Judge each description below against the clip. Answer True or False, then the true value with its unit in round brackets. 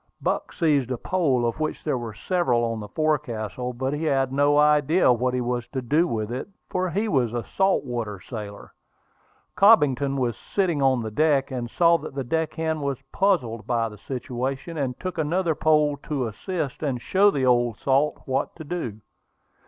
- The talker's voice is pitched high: False (135 Hz)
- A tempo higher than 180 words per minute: True (190 wpm)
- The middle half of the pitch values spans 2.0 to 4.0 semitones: False (4.6 semitones)